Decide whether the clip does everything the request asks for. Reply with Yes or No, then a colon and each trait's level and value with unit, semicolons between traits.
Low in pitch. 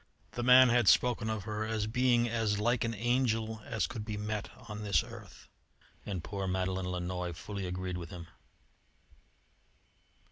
Yes: low, 105 Hz